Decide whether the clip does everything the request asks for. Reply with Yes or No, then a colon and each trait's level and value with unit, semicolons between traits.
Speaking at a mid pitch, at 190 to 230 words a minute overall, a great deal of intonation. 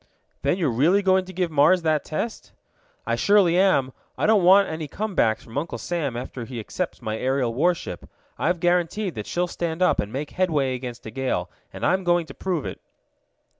Yes: medium, 165 Hz; average, 200 wpm; wide, 5.8 semitones